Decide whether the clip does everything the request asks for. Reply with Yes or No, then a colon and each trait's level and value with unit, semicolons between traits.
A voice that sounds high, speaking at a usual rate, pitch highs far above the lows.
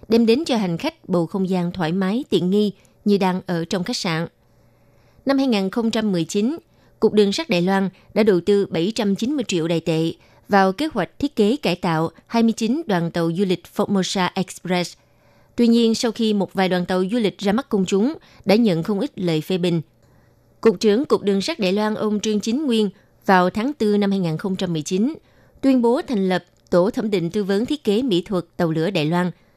No: high, 195 Hz; average, 205 wpm; average, 3.9 semitones